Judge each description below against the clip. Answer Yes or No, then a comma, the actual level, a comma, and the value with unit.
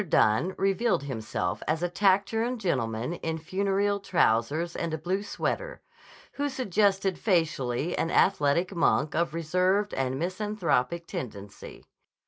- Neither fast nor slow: No, slow, 120 wpm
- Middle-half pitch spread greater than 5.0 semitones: Yes, wide, 5.5 semitones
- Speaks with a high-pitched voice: No, medium, 175 Hz